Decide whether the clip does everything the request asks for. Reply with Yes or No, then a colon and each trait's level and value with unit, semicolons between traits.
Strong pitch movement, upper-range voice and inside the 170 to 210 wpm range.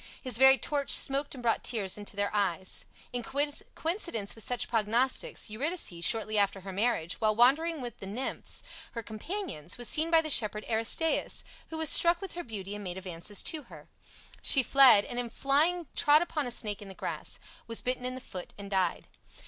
Yes: wide, 6.0 semitones; high, 240 Hz; average, 195 wpm